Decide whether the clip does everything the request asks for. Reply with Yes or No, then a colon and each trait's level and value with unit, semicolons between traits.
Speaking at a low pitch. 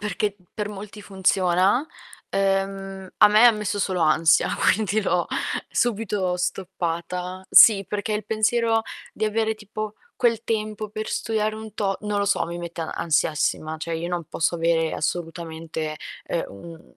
No: high, 195 Hz